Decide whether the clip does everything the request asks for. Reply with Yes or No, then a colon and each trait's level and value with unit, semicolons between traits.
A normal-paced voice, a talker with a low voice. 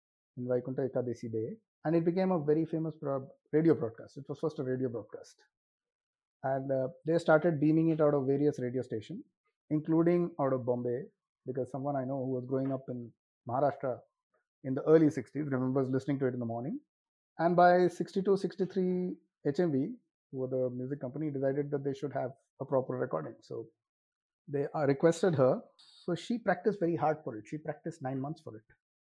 No: average, 180 wpm; medium, 150 Hz